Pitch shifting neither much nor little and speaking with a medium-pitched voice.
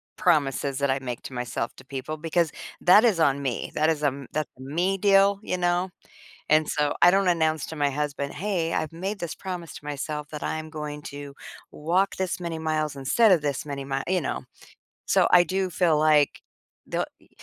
Yes: average, 3.8 semitones; medium, 155 Hz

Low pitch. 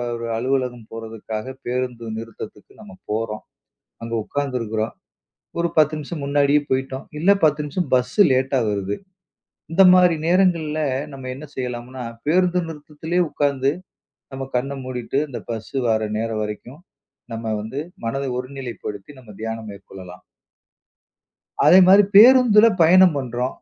Yes: low, 130 Hz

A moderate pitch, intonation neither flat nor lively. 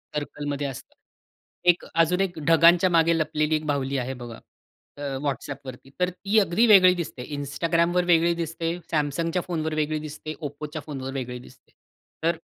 Yes: medium, 155 Hz; average, 3.1 semitones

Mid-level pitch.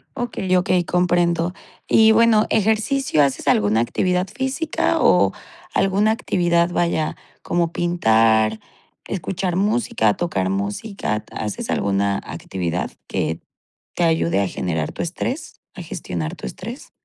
Yes: medium, 170 Hz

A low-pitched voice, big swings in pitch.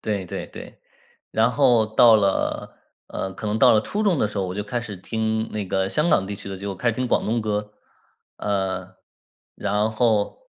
No: low, 105 Hz; average, 2.8 semitones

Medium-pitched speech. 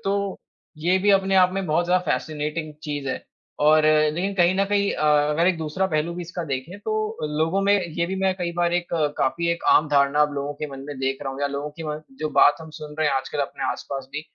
Yes: medium, 160 Hz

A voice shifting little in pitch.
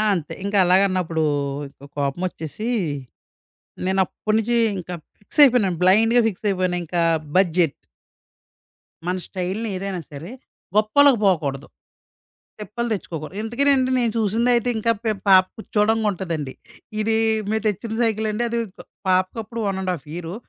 No: average, 3.8 semitones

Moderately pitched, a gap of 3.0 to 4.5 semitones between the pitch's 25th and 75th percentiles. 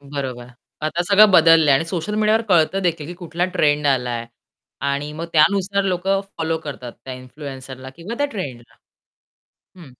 No: medium, 160 Hz; average, 5.1 semitones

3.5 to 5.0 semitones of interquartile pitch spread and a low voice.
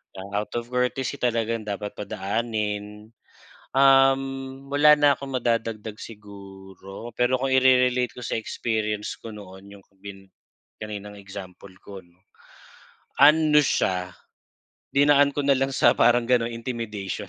Yes: average, 4.4 semitones; low, 115 Hz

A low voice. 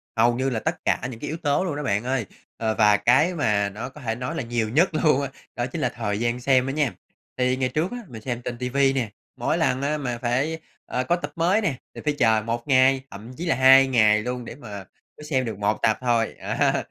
Yes: low, 125 Hz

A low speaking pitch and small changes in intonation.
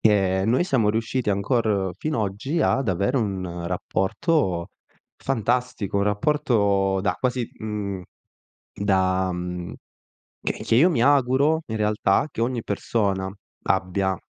No: low, 105 Hz; average, 4.7 semitones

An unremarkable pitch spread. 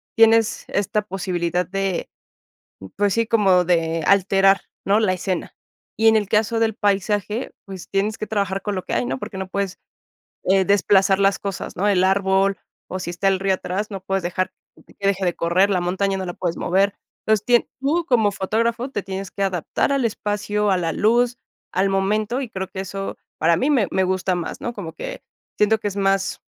No: narrow, 2.0 semitones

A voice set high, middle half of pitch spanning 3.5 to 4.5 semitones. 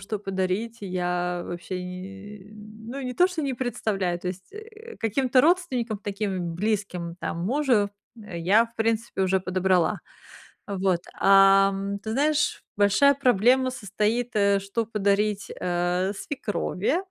Yes: high, 205 Hz; average, 3.9 semitones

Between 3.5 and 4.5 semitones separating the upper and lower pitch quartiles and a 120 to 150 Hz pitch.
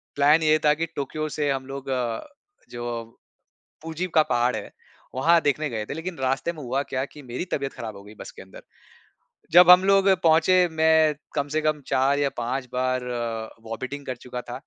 Yes: average, 3.9 semitones; medium, 140 Hz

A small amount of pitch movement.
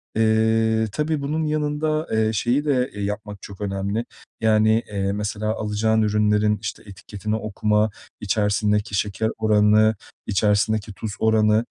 Yes: narrow, 1.3 semitones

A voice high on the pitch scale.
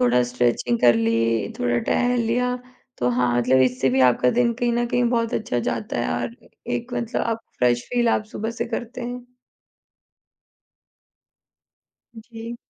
Yes: high, 220 Hz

